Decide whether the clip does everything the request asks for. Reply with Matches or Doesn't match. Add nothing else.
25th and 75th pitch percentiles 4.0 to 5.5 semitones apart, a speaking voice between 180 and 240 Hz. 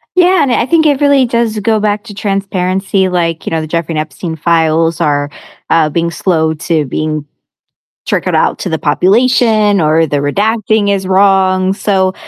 Matches